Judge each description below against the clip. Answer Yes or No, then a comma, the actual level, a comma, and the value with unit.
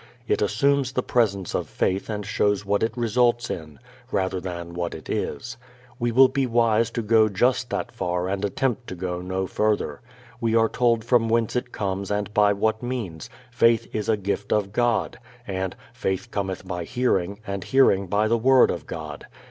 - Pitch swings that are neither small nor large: Yes, average, 3.8 semitones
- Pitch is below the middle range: Yes, low, 105 Hz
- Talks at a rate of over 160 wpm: Yes, average, 190 wpm